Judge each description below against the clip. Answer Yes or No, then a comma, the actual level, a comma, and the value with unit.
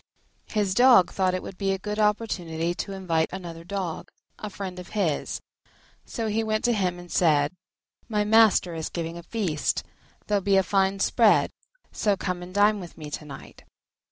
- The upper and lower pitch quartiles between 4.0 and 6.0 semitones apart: No, average, 3.4 semitones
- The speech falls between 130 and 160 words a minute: No, average, 185 wpm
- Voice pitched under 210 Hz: Yes, high, 190 Hz